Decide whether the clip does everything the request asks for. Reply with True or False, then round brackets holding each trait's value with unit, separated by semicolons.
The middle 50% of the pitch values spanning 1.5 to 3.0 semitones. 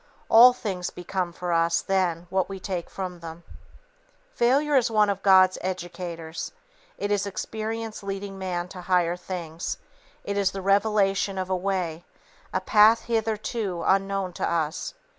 True (2.6 semitones)